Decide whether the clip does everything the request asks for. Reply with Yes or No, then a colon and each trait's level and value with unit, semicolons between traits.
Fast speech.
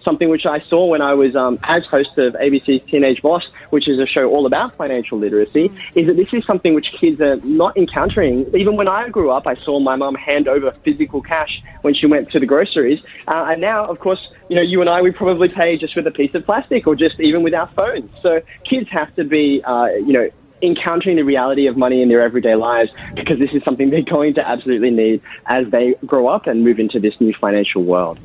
Yes: fast, 240 wpm